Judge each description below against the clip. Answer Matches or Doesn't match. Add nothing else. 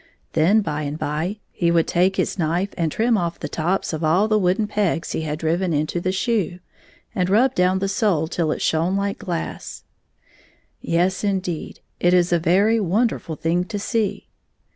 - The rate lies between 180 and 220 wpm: Matches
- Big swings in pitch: Doesn't match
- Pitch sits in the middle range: Matches